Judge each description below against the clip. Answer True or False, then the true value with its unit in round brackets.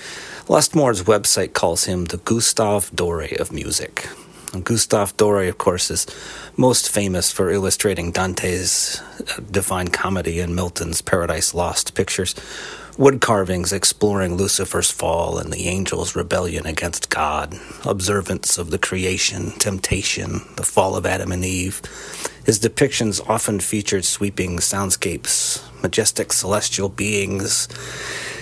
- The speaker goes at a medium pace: False (120 wpm)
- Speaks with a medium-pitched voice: False (95 Hz)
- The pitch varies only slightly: True (2.3 semitones)